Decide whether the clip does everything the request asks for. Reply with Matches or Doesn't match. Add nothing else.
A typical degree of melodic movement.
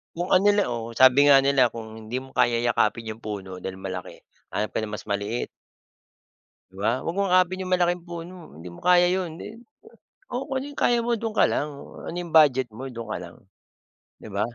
Doesn't match